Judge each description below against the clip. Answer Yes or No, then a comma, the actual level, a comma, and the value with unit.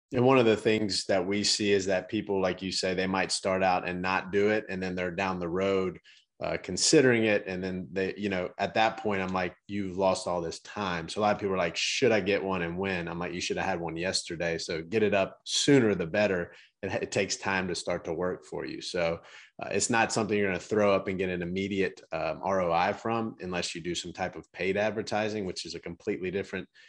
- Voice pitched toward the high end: No, very low, 95 Hz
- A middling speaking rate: No, fast, 255 wpm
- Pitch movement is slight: Yes, narrow, 2.3 semitones